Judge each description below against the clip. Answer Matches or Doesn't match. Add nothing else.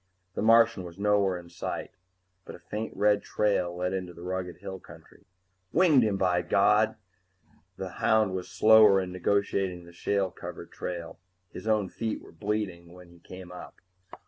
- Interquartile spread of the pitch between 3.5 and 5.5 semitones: Doesn't match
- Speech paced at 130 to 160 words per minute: Doesn't match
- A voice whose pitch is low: Matches